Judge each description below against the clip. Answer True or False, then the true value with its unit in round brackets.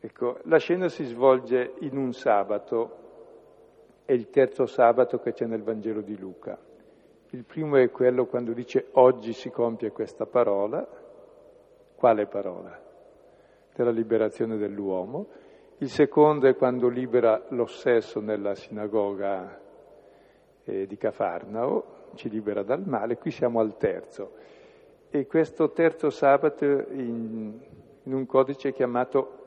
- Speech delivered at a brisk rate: False (125 wpm)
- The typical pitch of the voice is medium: False (130 Hz)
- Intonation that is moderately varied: False (6.2 semitones)